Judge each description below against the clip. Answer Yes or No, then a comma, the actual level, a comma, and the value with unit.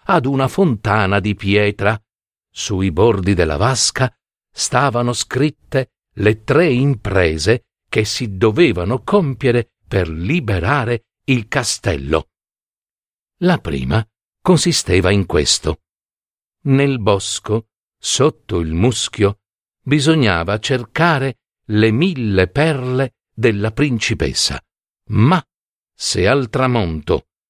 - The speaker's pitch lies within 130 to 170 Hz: No, low, 110 Hz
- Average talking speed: No, slow, 95 wpm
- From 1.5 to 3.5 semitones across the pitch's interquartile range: No, average, 4.9 semitones